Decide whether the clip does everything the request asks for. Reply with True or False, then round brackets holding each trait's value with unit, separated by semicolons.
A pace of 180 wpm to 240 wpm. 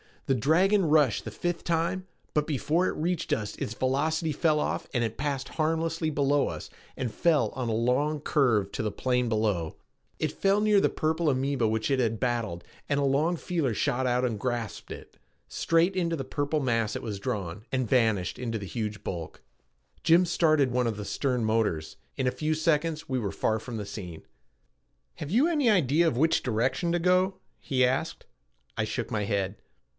True (190 wpm)